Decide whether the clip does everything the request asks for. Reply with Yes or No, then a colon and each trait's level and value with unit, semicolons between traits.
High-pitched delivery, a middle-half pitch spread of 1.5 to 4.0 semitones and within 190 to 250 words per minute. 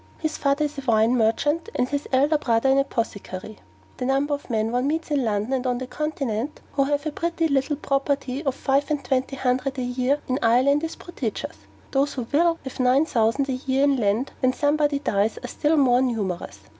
Yes: very high, 270 Hz; average, 2.7 semitones; fast, 205 wpm